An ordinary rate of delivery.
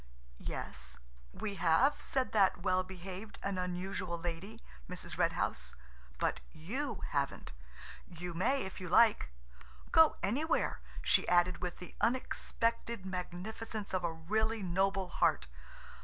No: slow, 120 wpm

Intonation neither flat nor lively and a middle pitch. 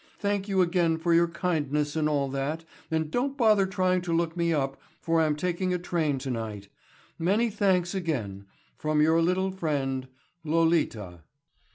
Yes: average, 3.7 semitones; medium, 165 Hz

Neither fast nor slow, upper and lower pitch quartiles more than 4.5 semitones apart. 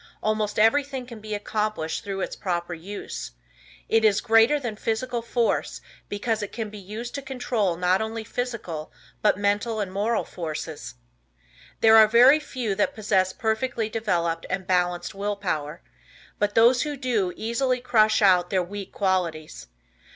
No: average, 155 wpm; average, 3.8 semitones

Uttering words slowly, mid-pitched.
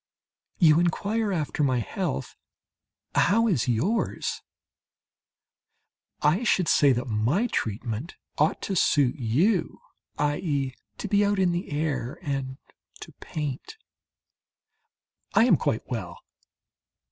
Yes: slow, 110 wpm; medium, 150 Hz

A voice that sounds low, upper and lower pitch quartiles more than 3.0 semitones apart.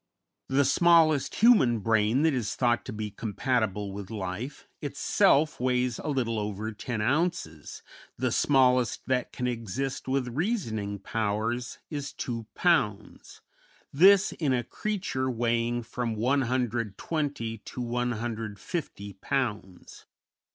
Yes: low, 120 Hz; average, 3.9 semitones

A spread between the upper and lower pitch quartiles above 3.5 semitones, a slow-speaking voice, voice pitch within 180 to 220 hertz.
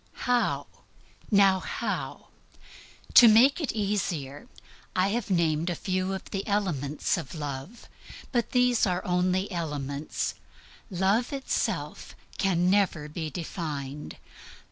Yes: average, 4.9 semitones; slow, 115 wpm; medium, 185 Hz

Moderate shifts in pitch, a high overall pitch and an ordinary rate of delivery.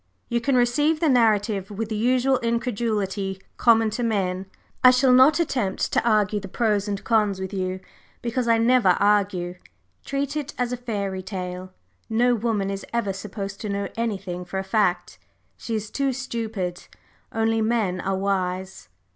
Yes: average, 3.7 semitones; high, 215 Hz; average, 165 wpm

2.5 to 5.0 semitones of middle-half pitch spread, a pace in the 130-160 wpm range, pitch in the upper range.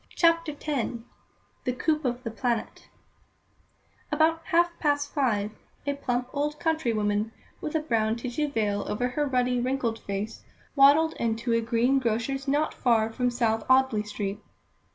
Yes: average, 4.4 semitones; average, 150 wpm; very high, 250 Hz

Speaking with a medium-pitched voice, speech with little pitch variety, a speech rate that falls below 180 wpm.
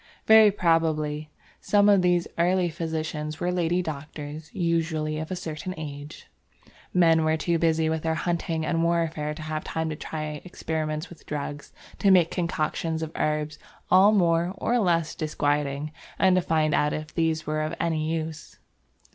Yes: medium, 160 Hz; narrow, 1.9 semitones; average, 165 wpm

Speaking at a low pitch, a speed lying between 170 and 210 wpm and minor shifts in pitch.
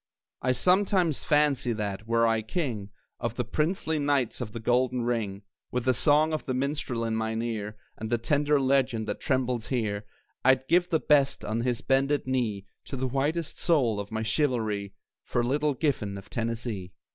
No: low, 125 Hz; average, 175 wpm; average, 4.4 semitones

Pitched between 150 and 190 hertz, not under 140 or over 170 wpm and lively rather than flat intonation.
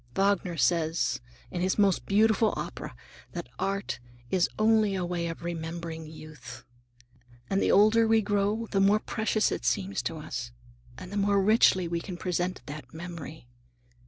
No: medium, 185 Hz; average, 160 wpm; average, 3.6 semitones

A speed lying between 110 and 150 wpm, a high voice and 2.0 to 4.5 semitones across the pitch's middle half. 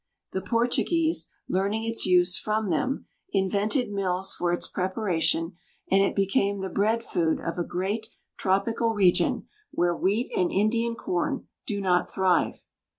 Yes: average, 145 wpm; high, 195 Hz; average, 3.5 semitones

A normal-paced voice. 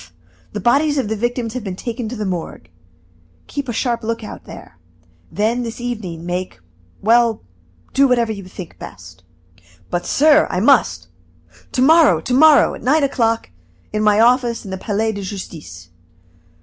Yes: average, 165 wpm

